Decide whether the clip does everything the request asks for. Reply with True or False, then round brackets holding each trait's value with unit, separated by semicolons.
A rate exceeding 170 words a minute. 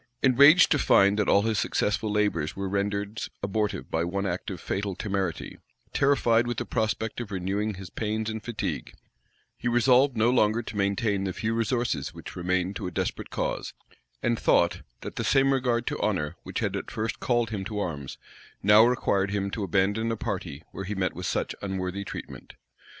True (190 wpm)